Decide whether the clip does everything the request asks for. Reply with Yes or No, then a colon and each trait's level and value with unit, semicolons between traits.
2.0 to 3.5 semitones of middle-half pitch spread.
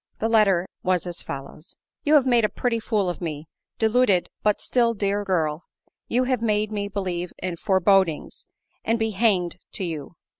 No: average, 4.0 semitones